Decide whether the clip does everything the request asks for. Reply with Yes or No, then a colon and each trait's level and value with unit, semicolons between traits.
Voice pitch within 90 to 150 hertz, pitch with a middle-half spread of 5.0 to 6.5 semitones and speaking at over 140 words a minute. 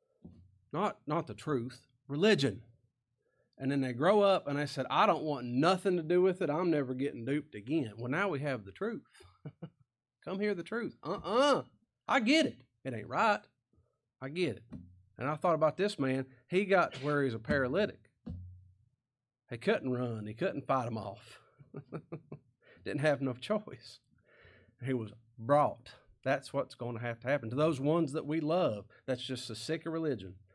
Yes: low, 135 Hz; average, 5.3 semitones; average, 185 wpm